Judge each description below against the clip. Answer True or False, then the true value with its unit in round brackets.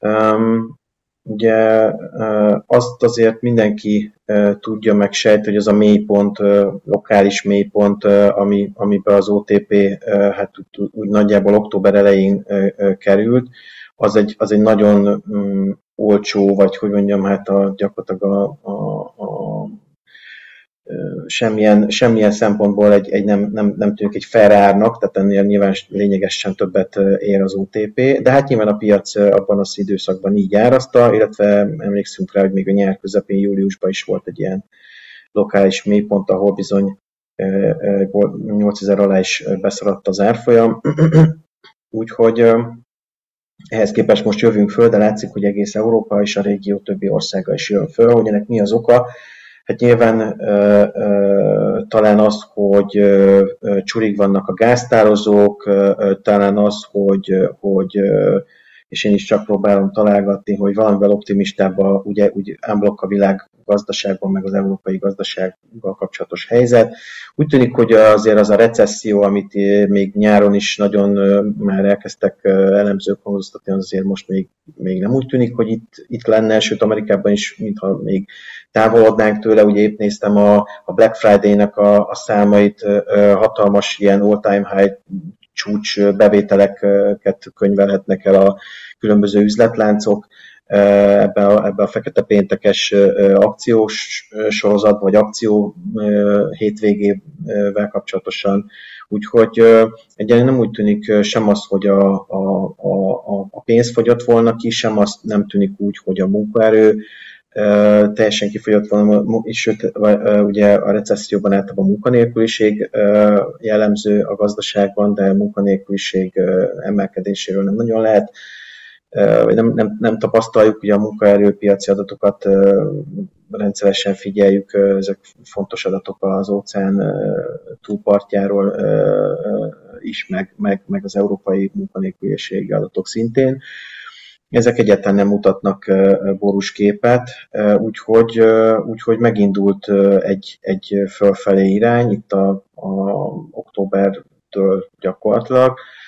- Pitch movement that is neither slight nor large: False (1.5 semitones)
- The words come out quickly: False (130 wpm)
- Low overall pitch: True (100 Hz)